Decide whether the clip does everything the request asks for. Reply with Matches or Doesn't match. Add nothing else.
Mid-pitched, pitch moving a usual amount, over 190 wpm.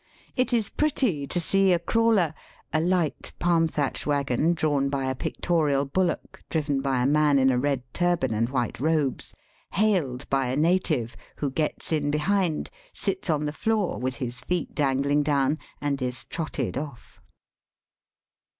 Doesn't match